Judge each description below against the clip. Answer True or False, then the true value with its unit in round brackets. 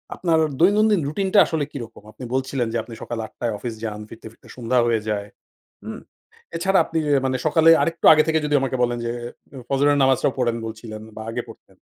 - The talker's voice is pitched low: True (130 Hz)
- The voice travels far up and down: True (5.7 semitones)